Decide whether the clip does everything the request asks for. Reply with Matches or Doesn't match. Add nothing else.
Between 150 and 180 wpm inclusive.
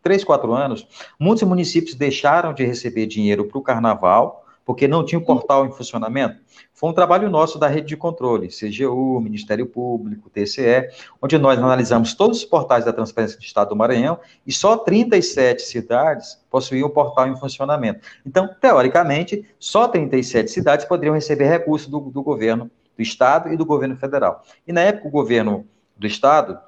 Matches